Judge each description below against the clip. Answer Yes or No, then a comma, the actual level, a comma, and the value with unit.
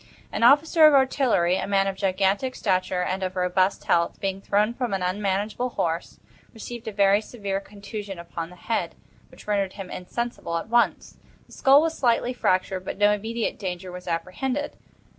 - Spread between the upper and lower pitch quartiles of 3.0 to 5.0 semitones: Yes, average, 4.1 semitones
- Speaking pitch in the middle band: No, high, 200 Hz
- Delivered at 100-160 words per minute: No, average, 175 wpm